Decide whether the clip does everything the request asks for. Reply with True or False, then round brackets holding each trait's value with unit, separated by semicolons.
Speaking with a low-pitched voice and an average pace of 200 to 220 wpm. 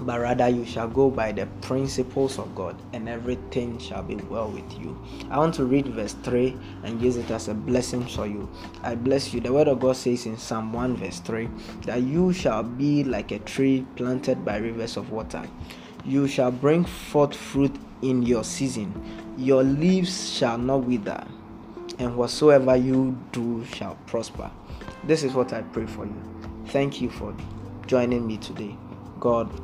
False (125 Hz; 180 wpm)